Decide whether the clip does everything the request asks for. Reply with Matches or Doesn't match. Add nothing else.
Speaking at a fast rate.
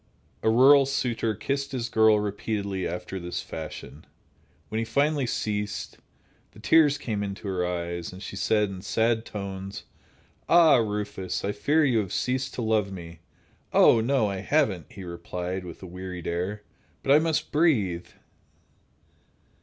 Doesn't match